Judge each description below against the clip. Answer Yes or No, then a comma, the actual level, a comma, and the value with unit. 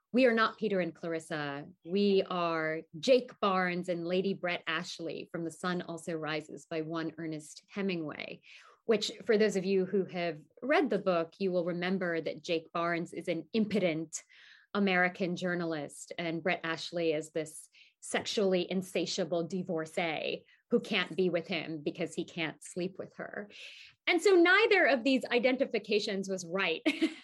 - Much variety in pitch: No, average, 3.6 semitones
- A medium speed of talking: No, fast, 155 wpm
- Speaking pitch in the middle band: Yes, medium, 180 Hz